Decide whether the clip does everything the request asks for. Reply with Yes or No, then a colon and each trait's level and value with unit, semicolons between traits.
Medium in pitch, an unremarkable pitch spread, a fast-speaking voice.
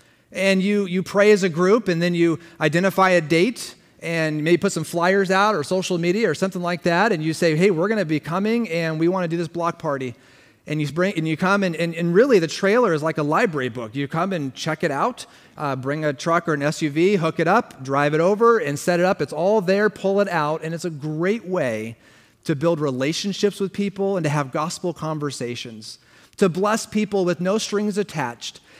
Yes: medium, 170 Hz; average, 4.1 semitones; fast, 230 wpm